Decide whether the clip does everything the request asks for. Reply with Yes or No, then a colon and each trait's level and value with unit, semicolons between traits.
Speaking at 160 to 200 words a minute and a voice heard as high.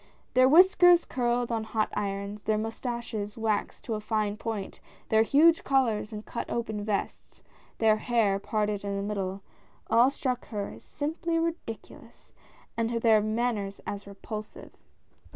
No: average, 145 wpm; high, 220 Hz